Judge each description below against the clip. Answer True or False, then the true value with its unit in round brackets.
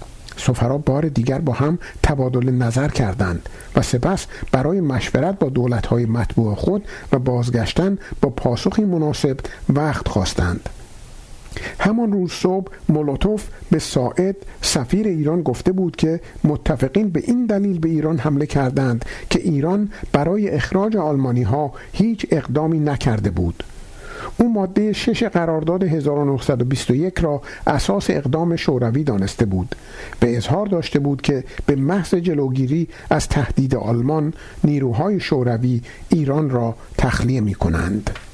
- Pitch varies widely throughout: True (6.3 semitones)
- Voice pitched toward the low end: False (145 Hz)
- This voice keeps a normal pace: True (125 wpm)